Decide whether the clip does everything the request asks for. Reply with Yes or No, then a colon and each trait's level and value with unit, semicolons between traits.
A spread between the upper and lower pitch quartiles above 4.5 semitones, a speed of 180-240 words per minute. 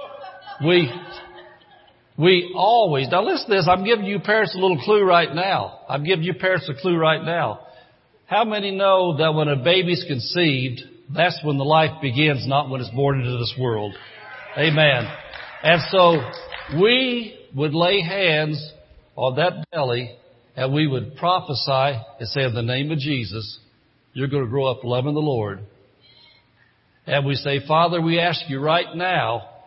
No: average, 5.1 semitones; average, 165 wpm